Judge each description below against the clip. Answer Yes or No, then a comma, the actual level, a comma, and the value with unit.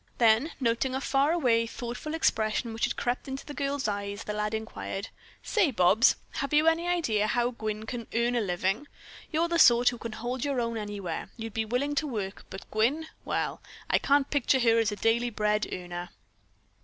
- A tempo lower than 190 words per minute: No, average, 195 wpm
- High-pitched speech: Yes, high, 235 Hz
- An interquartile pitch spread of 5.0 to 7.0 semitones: No, average, 4.1 semitones